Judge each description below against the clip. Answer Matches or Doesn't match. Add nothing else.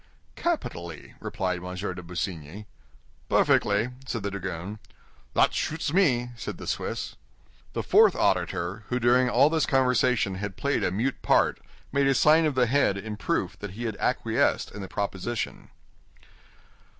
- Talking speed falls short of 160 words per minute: Matches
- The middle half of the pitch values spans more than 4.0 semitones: Matches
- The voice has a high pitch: Doesn't match